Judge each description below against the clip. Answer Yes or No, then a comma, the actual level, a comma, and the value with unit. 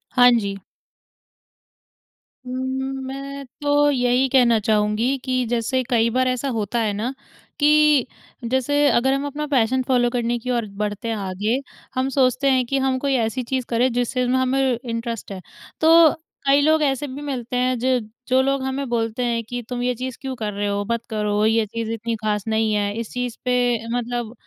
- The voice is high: Yes, high, 245 Hz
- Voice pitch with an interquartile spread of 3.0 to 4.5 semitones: No, narrow, 2.6 semitones